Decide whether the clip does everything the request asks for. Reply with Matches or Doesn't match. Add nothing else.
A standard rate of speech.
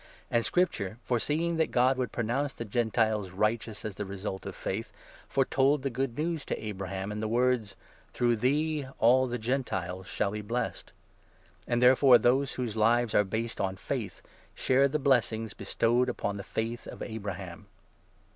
Matches